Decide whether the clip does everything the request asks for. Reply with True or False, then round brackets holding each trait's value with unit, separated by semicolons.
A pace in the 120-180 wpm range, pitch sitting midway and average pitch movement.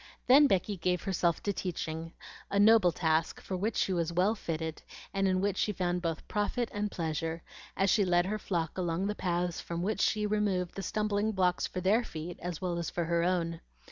False (205 wpm; 180 Hz; 3.2 semitones)